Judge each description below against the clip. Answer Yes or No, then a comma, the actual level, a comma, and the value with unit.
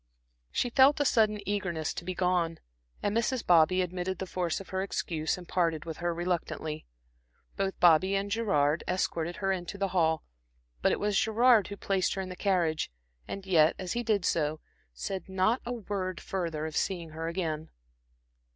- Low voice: No, medium, 185 Hz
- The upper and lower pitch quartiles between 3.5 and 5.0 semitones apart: No, average, 3.1 semitones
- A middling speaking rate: Yes, average, 180 wpm